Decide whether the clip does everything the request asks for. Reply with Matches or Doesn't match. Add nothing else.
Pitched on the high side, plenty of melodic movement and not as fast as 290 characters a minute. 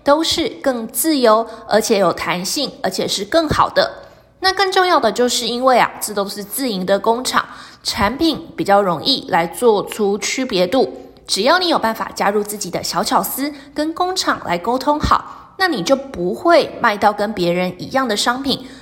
Matches